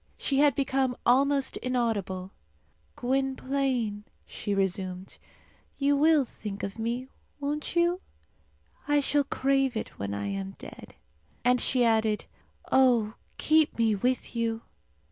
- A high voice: Yes, very high, 250 Hz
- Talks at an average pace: No, slow, 125 wpm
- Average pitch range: Yes, average, 4.7 semitones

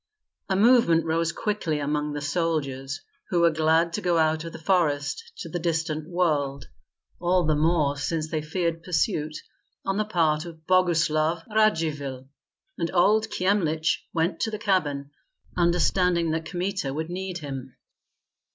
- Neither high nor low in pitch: Yes, medium, 165 Hz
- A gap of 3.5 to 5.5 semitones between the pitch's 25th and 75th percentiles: No, average, 2.7 semitones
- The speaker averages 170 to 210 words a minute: No, average, 150 wpm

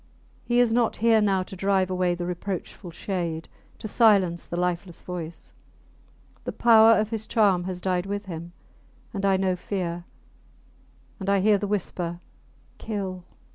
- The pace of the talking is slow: No, average, 155 wpm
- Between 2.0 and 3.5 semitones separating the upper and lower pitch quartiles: Yes, average, 2.8 semitones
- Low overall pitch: No, high, 190 Hz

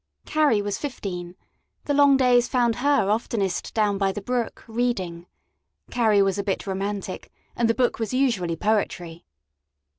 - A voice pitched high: Yes, high, 215 Hz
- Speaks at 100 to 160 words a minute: Yes, average, 150 wpm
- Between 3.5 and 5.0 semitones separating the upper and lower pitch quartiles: Yes, average, 4.1 semitones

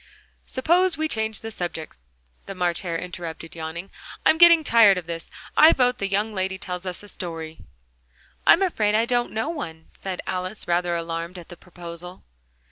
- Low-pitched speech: No, medium, 185 Hz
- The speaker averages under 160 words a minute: No, average, 175 wpm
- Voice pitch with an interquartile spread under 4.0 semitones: No, average, 4.6 semitones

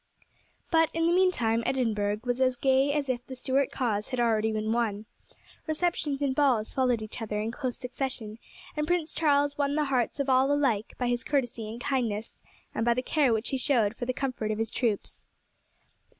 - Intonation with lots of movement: No, average, 3.9 semitones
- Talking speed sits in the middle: Yes, average, 195 wpm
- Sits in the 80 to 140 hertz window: No, very high, 255 Hz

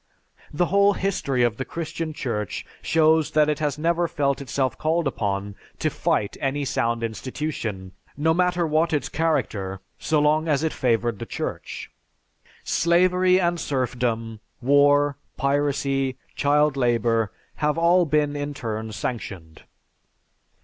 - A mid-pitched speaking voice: Yes, medium, 145 Hz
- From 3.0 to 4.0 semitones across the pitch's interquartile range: No, average, 5.1 semitones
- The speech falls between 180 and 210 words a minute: No, slow, 135 wpm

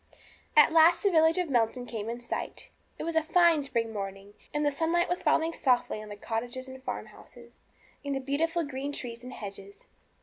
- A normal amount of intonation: No, wide, 5.8 semitones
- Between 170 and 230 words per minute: Yes, average, 195 wpm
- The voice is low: No, very high, 270 Hz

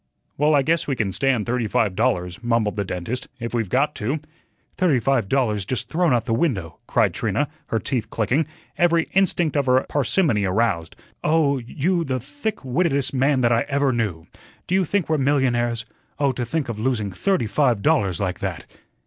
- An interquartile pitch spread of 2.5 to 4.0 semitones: No, average, 4.9 semitones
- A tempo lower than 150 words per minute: No, average, 190 wpm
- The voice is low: Yes, low, 125 Hz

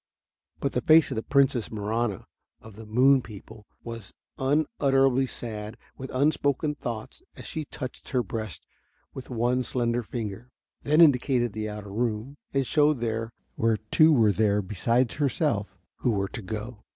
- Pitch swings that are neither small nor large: Yes, average, 3.8 semitones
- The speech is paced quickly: No, average, 150 wpm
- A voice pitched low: Yes, low, 120 Hz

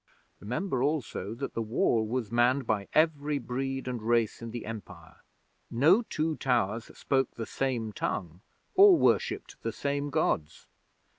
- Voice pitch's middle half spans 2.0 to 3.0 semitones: No, average, 4.2 semitones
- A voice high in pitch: No, low, 125 Hz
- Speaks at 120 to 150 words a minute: Yes, average, 145 wpm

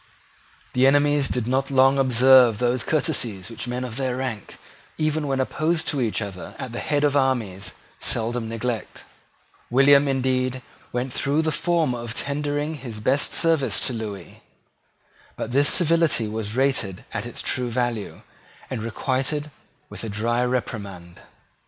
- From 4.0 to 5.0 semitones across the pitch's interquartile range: No, average, 3.5 semitones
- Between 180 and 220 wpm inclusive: No, average, 150 wpm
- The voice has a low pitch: Yes, low, 130 Hz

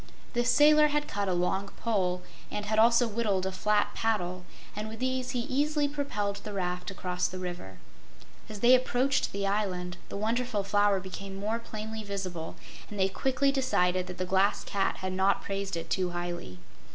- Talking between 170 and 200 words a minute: Yes, average, 180 wpm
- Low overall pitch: No, high, 200 Hz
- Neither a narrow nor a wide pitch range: Yes, average, 4.1 semitones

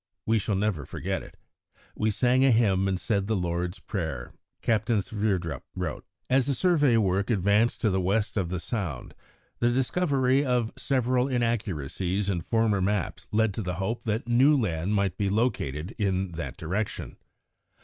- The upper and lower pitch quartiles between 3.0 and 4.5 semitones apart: Yes, average, 4.2 semitones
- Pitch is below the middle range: Yes, low, 105 Hz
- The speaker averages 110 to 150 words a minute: No, average, 165 wpm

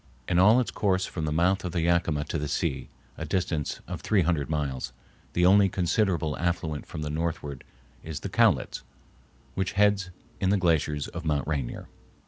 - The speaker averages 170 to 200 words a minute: Yes, average, 180 wpm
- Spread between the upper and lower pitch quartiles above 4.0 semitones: No, average, 3.7 semitones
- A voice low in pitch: Yes, very low, 85 Hz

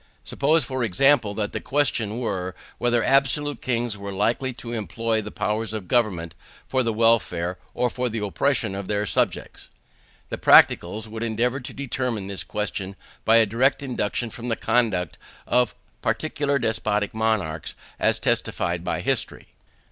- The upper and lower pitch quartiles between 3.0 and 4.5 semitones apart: Yes, average, 3.4 semitones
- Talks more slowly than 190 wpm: Yes, average, 155 wpm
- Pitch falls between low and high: No, low, 115 Hz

